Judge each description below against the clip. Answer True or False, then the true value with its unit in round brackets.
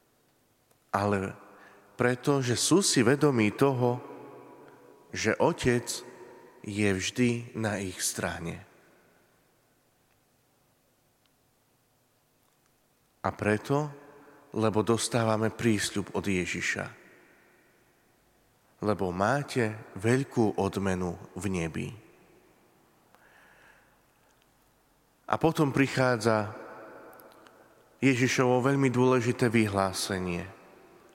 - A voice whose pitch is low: True (115 Hz)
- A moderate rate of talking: False (65 wpm)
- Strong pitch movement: False (3.8 semitones)